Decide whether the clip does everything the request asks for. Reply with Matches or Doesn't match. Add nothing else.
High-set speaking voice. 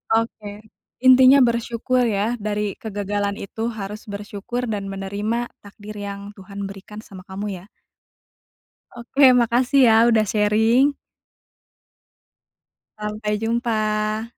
Matches